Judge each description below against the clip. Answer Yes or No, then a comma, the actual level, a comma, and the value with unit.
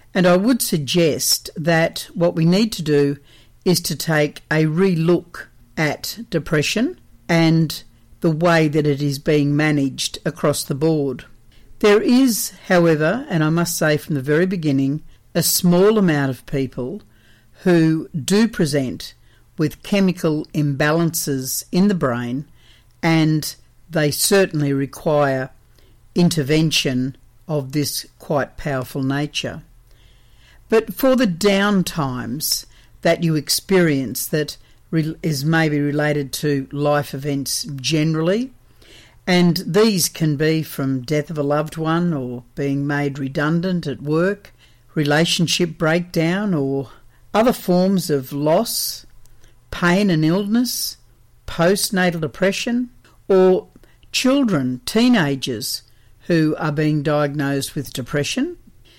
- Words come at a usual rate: No, slow, 115 wpm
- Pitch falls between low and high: Yes, medium, 155 Hz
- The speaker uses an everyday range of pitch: Yes, average, 4.2 semitones